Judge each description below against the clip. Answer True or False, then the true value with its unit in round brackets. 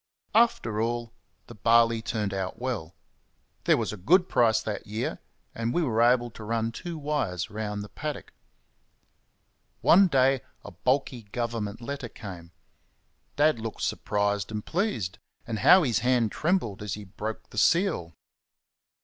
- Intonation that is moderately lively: True (4.2 semitones)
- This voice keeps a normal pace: True (150 wpm)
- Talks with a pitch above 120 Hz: False (115 Hz)